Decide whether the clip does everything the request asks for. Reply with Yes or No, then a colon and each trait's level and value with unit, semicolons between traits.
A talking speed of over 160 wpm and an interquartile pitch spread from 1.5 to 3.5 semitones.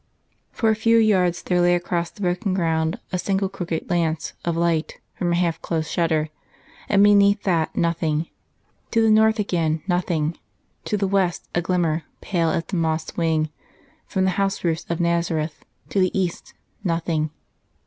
Yes: average, 170 wpm; average, 2.9 semitones